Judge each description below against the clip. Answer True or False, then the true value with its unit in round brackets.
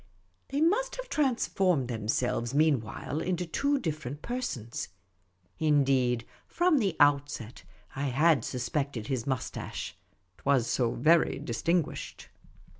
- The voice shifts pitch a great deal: True (6.4 semitones)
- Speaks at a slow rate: True (120 wpm)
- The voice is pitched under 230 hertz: True (140 Hz)